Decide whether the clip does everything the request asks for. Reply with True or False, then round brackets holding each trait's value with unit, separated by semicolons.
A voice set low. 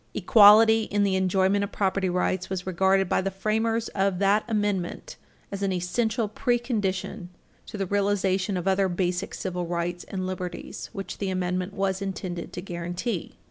False (195 Hz)